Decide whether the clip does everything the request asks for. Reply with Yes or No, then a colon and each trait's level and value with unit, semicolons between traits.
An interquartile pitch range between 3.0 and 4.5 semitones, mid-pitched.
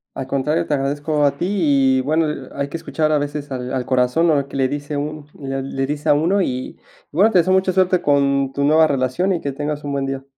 No: narrow, 2.6 semitones; medium, 145 Hz